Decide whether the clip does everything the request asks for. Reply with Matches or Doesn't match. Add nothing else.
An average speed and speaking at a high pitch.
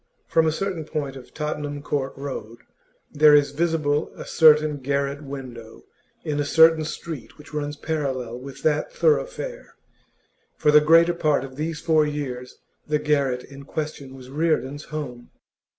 Doesn't match